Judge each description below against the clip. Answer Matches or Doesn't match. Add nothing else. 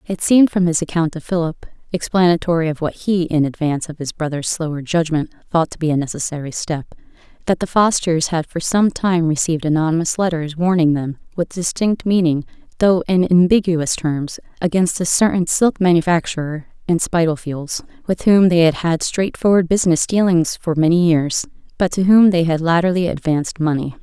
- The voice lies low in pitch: Doesn't match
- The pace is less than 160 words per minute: Doesn't match